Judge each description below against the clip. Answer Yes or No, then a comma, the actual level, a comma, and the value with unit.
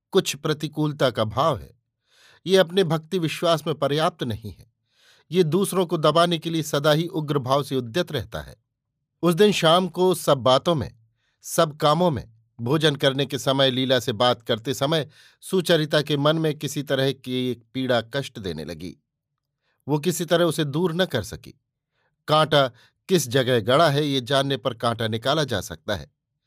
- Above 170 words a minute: Yes, average, 180 wpm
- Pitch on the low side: No, medium, 145 Hz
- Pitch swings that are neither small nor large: Yes, average, 4.4 semitones